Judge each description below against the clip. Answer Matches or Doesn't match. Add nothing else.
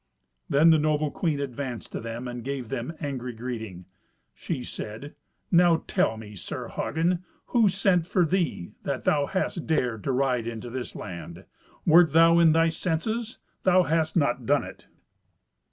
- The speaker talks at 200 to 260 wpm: Doesn't match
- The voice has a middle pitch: Matches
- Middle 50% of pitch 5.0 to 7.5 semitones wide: Matches